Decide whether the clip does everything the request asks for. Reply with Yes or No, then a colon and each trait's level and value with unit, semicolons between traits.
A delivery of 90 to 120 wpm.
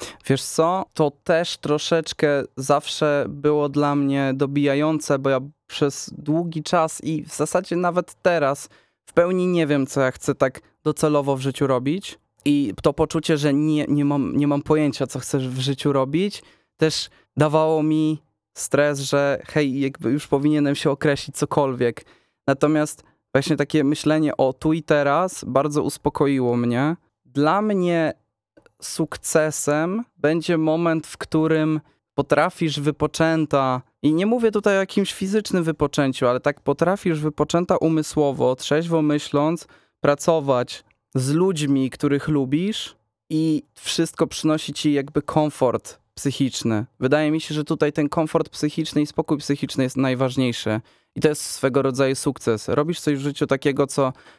No: average, 145 wpm